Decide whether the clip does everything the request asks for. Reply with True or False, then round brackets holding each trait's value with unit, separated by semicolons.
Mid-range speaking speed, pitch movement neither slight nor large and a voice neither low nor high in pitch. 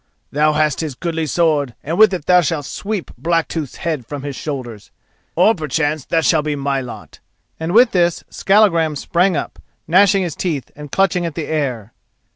True (175 wpm; 3.3 semitones; 160 Hz)